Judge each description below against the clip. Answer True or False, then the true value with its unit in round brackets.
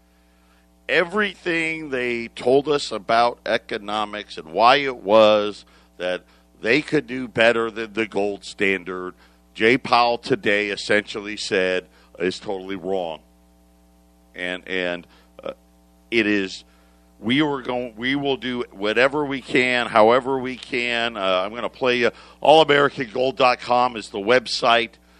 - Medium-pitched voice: False (105 Hz)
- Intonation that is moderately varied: False (6.2 semitones)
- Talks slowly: True (130 wpm)